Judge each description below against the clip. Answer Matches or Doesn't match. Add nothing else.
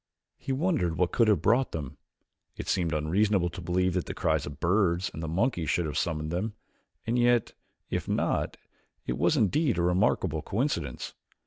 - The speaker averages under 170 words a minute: Doesn't match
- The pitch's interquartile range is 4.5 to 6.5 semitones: Matches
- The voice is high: Doesn't match